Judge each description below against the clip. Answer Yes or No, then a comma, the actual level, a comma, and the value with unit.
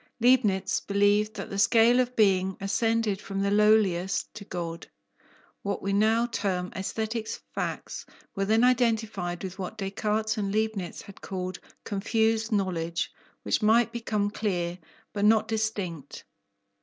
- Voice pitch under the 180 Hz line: No, high, 205 Hz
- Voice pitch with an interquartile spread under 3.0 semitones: Yes, narrow, 2.5 semitones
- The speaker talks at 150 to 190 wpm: No, slow, 135 wpm